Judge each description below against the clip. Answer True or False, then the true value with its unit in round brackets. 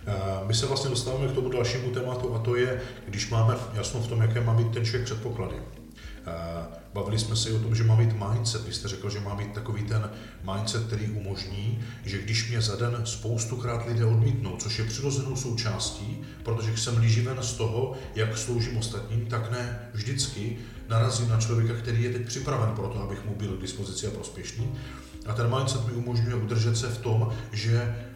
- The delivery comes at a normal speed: False (195 wpm)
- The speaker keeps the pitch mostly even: True (2.0 semitones)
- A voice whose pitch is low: True (115 Hz)